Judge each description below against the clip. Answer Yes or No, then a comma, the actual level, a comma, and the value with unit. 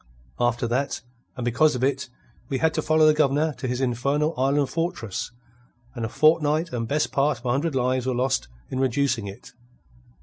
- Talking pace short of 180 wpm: No, average, 190 wpm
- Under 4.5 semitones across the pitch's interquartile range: Yes, average, 3.6 semitones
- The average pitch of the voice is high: No, low, 135 Hz